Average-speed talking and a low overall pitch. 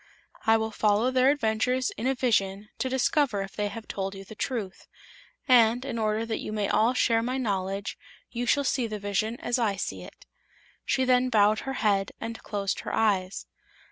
No: average, 195 wpm; high, 220 Hz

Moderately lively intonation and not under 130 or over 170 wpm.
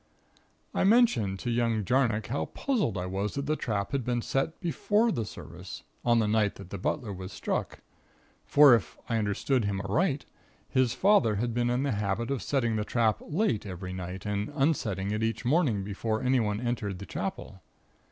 No: average, 4.8 semitones; average, 185 wpm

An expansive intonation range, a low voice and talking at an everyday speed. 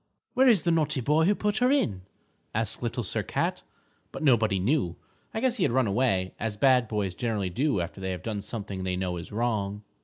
No: wide, 7.0 semitones; low, 110 Hz; fast, 215 wpm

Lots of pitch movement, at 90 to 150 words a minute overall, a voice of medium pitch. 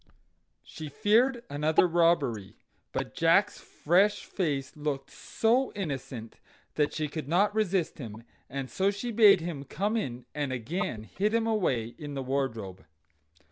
Yes: wide, 7.2 semitones; average, 140 wpm; medium, 155 Hz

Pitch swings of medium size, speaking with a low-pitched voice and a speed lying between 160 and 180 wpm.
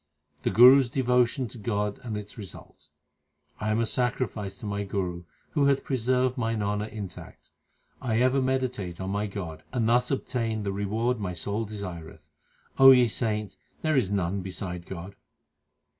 Yes: average, 4.0 semitones; low, 110 Hz; average, 165 wpm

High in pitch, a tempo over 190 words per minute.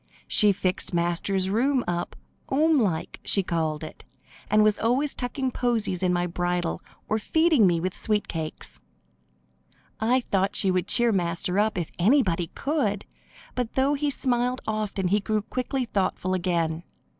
No: high, 205 Hz; average, 150 wpm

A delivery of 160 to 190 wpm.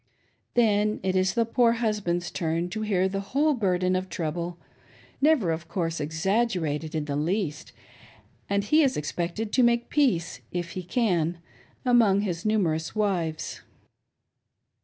No: average, 150 wpm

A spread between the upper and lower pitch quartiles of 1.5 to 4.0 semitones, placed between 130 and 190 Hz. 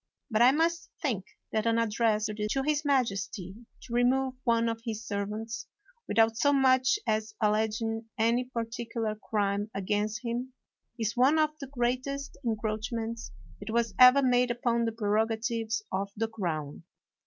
No: narrow, 2.6 semitones; high, 230 Hz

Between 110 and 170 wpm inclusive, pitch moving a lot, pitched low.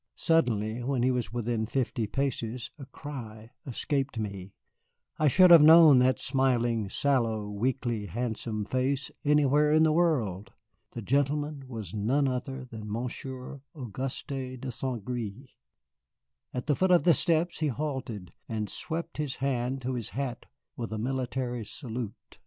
No: average, 145 wpm; average, 3.6 semitones; low, 125 Hz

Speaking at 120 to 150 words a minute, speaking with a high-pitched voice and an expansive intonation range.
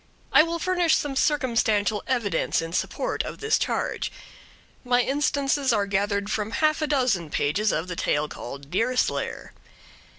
Yes: average, 145 wpm; high, 235 Hz; wide, 6.4 semitones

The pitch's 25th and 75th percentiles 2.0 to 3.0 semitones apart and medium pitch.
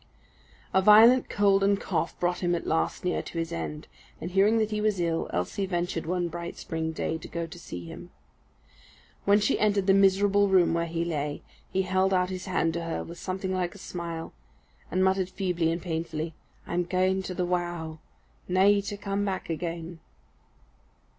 Yes: narrow, 2.6 semitones; medium, 180 Hz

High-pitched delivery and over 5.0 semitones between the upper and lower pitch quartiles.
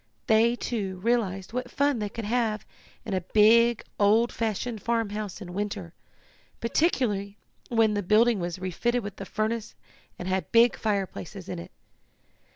No: high, 215 Hz; average, 3.1 semitones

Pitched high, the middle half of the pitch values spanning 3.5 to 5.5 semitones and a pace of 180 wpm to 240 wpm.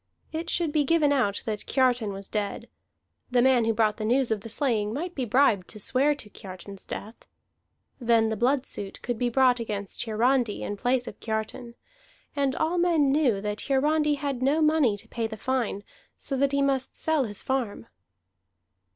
Yes: high, 245 Hz; average, 4.4 semitones; average, 185 wpm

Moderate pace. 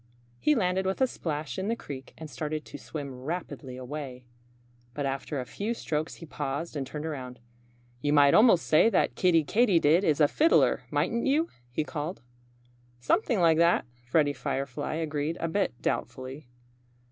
Yes: average, 165 wpm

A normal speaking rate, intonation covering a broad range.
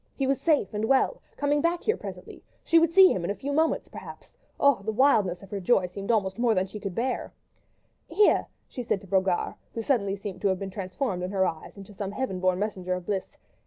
No: fast, 235 wpm; wide, 5.9 semitones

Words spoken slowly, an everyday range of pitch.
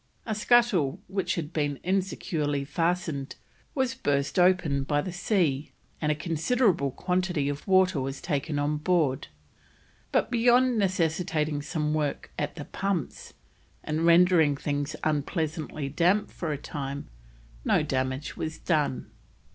Yes: slow, 130 wpm; average, 4.2 semitones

